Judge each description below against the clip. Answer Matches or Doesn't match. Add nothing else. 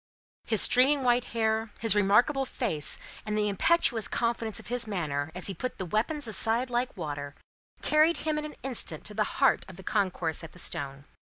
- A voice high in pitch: Matches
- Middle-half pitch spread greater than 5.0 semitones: Matches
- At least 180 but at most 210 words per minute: Matches